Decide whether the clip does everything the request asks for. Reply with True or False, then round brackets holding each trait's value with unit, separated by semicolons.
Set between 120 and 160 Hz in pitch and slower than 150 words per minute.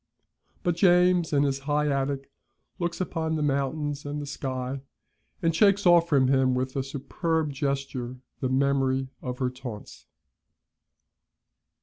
True (140 Hz; 135 wpm)